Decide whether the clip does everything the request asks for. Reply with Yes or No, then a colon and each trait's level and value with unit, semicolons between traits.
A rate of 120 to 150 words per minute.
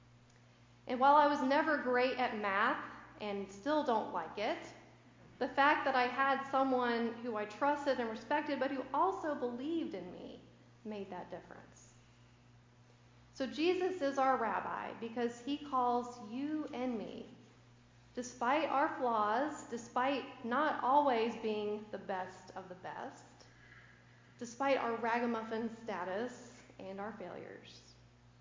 Yes: slow, 135 wpm